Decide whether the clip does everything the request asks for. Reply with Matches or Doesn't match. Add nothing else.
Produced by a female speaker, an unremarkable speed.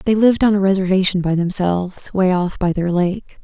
Doesn't match